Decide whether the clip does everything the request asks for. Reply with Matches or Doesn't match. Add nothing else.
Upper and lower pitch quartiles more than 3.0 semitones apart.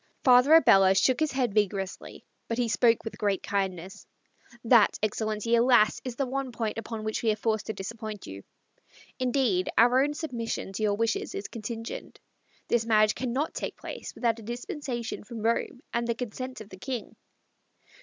Doesn't match